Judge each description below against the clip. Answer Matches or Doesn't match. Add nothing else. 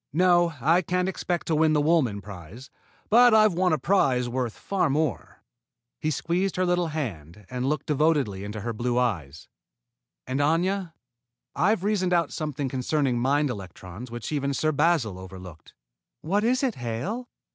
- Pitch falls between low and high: Matches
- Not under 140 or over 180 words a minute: Matches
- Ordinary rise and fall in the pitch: Doesn't match